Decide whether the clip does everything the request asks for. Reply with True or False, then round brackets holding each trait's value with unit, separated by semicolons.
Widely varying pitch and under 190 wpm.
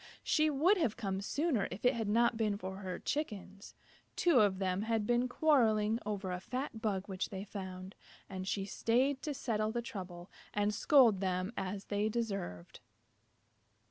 False (3.8 semitones; 170 wpm)